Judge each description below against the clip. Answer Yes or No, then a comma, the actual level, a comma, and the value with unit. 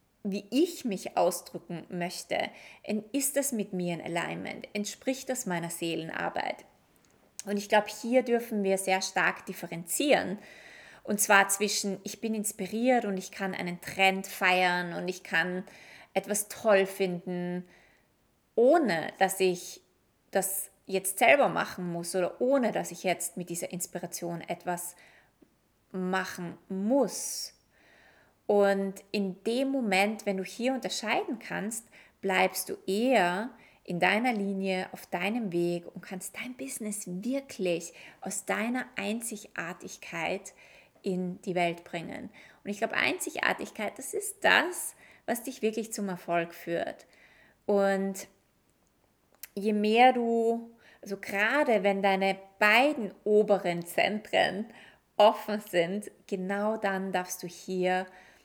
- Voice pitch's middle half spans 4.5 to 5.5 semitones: No, average, 2.9 semitones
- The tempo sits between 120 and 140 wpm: Yes, slow, 125 wpm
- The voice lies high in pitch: Yes, high, 195 Hz